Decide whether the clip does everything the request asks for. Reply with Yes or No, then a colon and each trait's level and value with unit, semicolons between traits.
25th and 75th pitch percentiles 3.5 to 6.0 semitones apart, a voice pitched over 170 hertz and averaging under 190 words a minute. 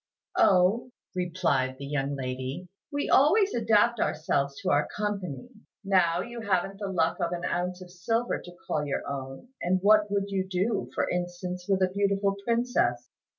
Yes: average, 4.1 semitones; medium, 185 Hz; average, 165 wpm